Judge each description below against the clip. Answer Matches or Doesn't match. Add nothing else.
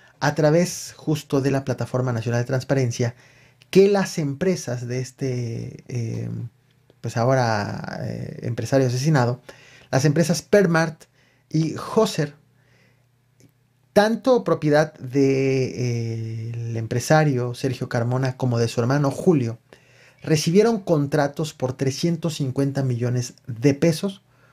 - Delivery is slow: Matches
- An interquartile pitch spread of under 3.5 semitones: Doesn't match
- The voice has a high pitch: Doesn't match